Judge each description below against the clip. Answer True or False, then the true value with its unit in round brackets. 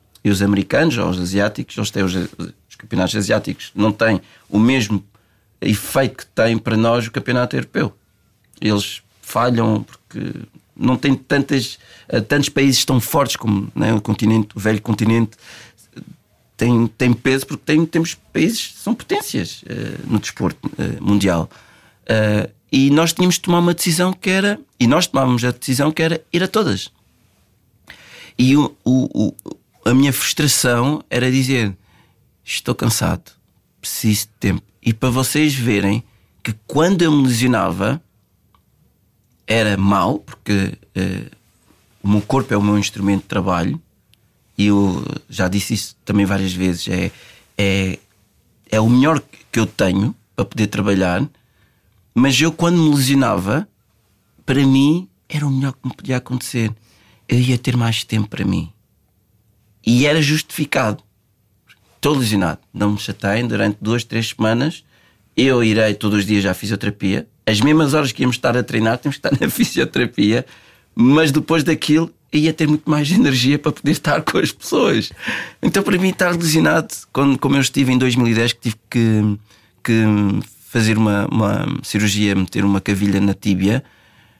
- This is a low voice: True (115 Hz)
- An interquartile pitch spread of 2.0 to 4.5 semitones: False (5.1 semitones)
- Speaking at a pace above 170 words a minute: False (155 wpm)